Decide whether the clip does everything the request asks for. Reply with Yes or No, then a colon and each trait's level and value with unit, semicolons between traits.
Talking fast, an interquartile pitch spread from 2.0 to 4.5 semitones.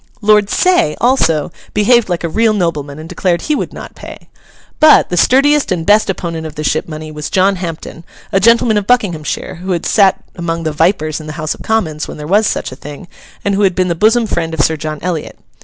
No: fast, 225 wpm; average, 5.0 semitones